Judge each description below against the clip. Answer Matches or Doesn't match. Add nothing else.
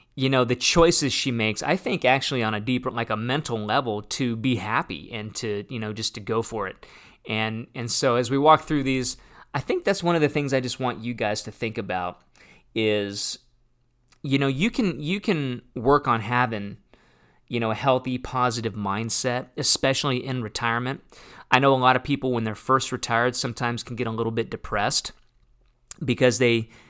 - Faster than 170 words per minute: Matches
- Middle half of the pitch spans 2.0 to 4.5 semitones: Matches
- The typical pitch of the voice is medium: Doesn't match